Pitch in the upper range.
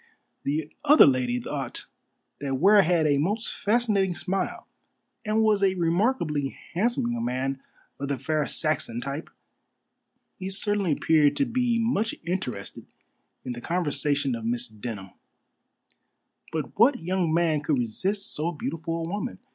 No: medium, 165 Hz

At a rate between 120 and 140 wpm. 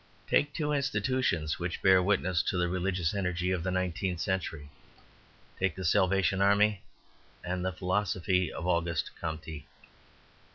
Yes: slow, 135 wpm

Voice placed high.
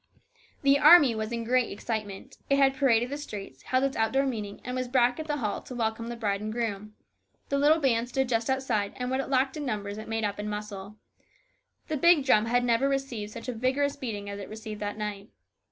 Yes: high, 235 Hz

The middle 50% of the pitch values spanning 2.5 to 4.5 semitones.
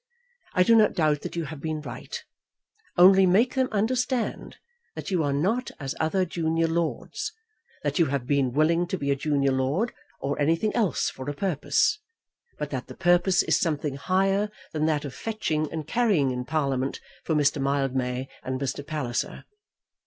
No: average, 5.2 semitones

